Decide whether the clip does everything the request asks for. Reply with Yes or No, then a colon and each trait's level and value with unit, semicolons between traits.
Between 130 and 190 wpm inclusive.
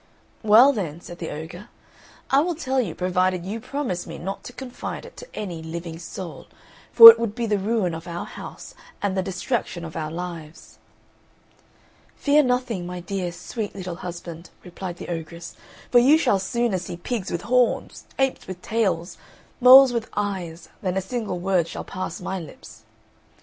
Yes: average, 175 wpm